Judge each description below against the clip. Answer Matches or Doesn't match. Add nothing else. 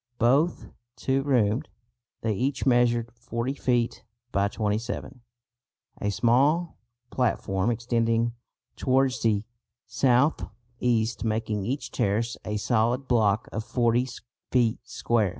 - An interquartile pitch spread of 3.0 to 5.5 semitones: Doesn't match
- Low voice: Matches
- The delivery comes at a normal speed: Doesn't match